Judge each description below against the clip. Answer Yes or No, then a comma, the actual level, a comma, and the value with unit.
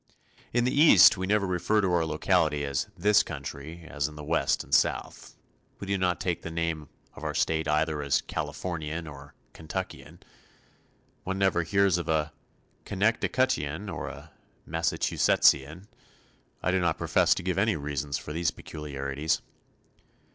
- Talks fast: No, average, 155 wpm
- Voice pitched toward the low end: Yes, very low, 80 Hz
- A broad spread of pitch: No, average, 3.8 semitones